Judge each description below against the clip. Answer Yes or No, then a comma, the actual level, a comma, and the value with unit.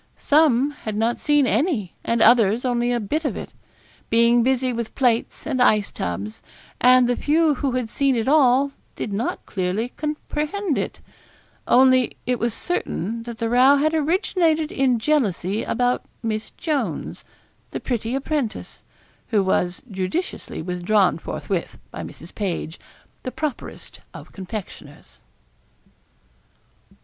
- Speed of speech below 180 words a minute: Yes, slow, 135 wpm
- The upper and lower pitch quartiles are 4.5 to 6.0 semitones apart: Yes, average, 4.8 semitones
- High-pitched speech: Yes, high, 245 Hz